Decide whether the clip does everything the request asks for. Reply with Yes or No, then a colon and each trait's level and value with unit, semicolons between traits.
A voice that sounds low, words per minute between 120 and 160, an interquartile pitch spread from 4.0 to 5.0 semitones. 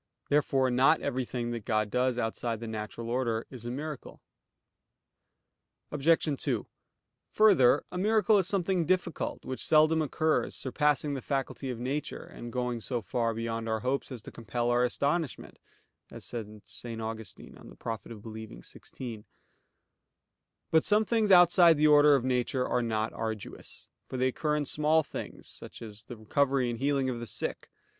Yes: low, 130 Hz; average, 155 wpm; average, 4.5 semitones